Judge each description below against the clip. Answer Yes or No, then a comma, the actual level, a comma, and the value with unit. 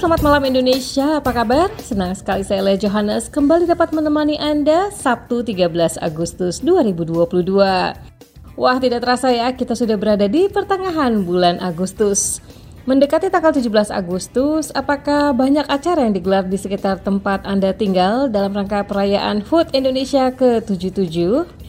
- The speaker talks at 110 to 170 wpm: Yes, average, 135 wpm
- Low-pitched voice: No, high, 240 Hz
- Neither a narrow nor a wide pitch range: No, wide, 6.8 semitones